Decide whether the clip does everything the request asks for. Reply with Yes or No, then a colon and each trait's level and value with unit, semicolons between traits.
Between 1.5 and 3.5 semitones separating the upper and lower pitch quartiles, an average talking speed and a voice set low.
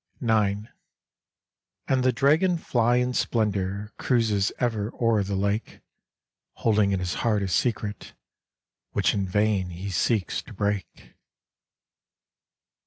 No: average, 3.2 semitones; slow, 110 wpm; low, 105 Hz